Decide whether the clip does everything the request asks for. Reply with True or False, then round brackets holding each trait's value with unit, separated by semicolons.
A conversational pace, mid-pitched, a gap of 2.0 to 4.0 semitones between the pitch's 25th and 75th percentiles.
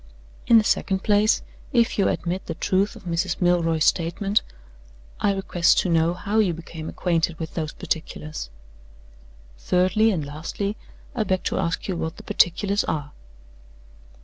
True (150 wpm; 180 Hz; 3.5 semitones)